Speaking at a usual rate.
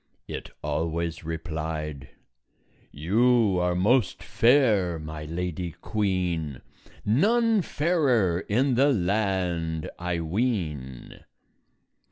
No: slow, 85 wpm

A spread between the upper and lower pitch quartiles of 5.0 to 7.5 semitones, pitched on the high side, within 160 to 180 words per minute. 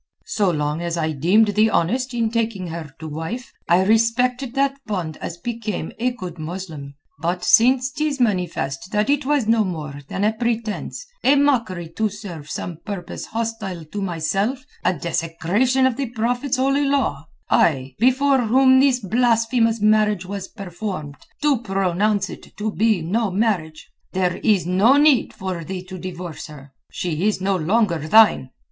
Yes: wide, 5.5 semitones; high, 205 Hz; average, 165 wpm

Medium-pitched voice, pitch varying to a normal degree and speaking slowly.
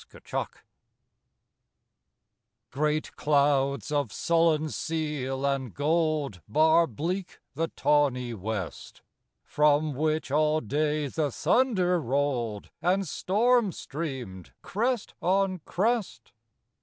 Yes: medium, 150 Hz; average, 3.8 semitones; slow, 95 wpm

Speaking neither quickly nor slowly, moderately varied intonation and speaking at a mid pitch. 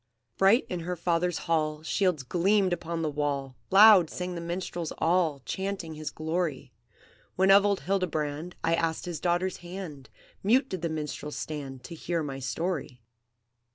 Yes: average, 155 wpm; average, 3.2 semitones; medium, 170 Hz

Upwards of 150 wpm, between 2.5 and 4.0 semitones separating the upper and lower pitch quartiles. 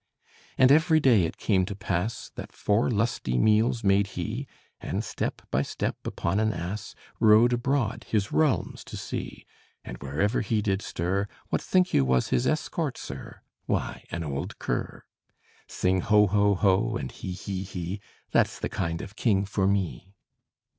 Yes: average, 165 wpm; average, 3.3 semitones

